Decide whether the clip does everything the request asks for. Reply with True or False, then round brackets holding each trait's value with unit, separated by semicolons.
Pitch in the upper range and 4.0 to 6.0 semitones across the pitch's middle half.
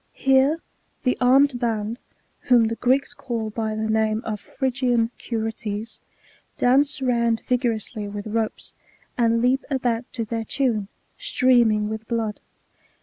False (230 Hz; 2.4 semitones)